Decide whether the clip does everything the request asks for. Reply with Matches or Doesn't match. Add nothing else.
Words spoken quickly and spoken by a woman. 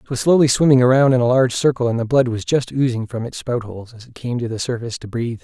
Doesn't match